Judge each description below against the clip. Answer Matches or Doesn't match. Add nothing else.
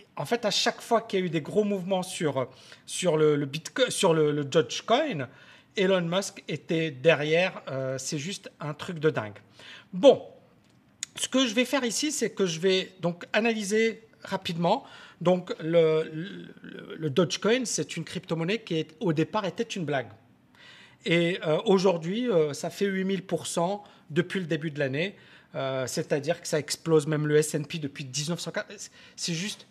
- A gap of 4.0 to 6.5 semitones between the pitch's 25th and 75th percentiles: Matches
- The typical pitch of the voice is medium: Matches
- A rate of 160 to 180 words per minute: Matches